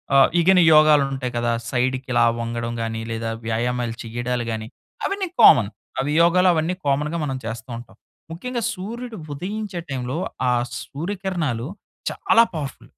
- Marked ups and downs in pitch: Yes, wide, 7.1 semitones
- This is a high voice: No, low, 135 Hz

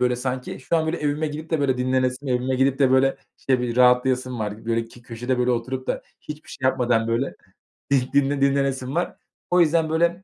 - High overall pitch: No, low, 130 Hz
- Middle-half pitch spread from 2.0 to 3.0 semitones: Yes, narrow, 2.5 semitones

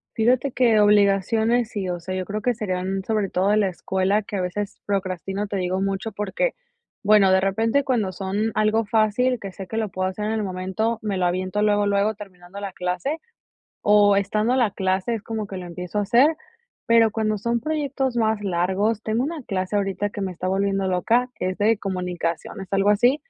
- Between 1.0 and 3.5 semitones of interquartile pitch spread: Yes, average, 2.9 semitones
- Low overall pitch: No, high, 205 Hz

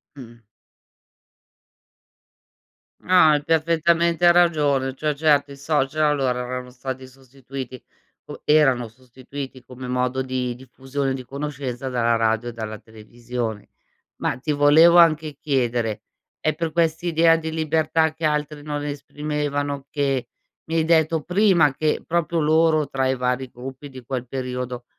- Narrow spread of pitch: No, average, 3.6 semitones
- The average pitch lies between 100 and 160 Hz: Yes, medium, 140 Hz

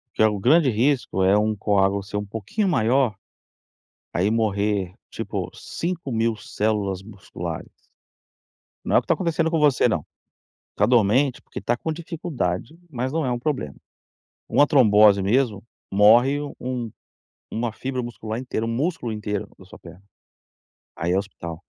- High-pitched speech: No, low, 115 Hz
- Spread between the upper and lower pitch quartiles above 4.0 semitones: Yes, average, 4.7 semitones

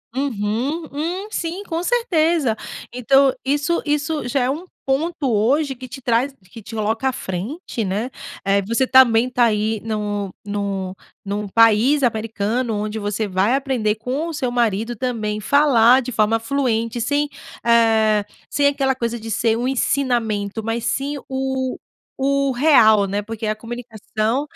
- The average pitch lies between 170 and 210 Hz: No, high, 240 Hz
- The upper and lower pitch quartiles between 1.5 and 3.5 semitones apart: No, average, 4.2 semitones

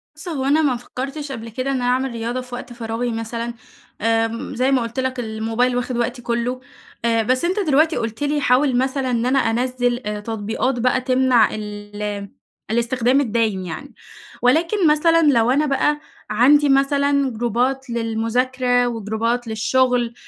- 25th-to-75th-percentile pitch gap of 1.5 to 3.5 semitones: Yes, average, 2.8 semitones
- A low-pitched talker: No, high, 245 Hz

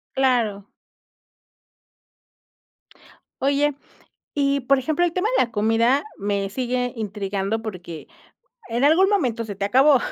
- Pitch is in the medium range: No, high, 245 Hz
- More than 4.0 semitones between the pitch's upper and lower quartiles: Yes, average, 5.2 semitones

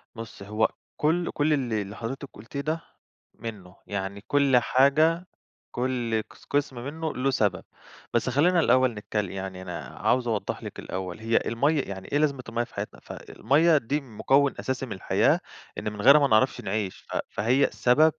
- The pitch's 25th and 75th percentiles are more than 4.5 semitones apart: Yes, average, 5.1 semitones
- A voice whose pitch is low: Yes, low, 125 Hz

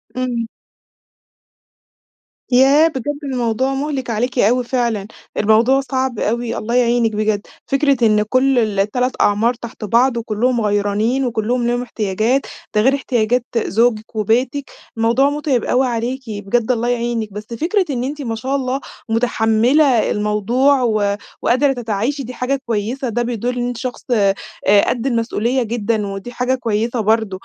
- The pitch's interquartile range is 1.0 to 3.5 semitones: Yes, average, 2.9 semitones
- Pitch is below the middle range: No, high, 240 Hz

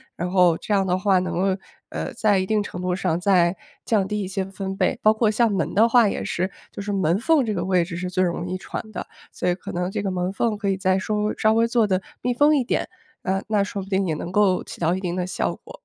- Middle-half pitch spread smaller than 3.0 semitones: Yes, narrow, 2.5 semitones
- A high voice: Yes, high, 195 Hz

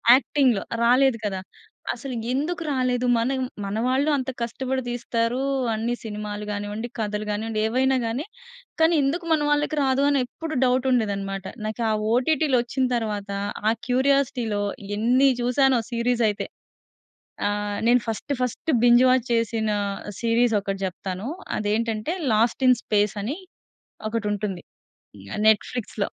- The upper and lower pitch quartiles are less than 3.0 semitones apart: No, average, 3.5 semitones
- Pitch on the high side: Yes, high, 240 Hz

